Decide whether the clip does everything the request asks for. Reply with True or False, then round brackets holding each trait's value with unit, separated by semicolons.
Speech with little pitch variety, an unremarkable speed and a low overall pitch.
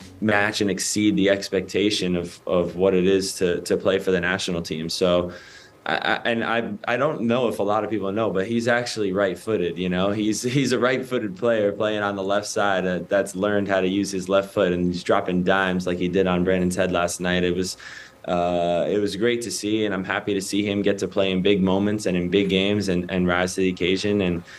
False (2.2 semitones; 235 wpm; 95 Hz)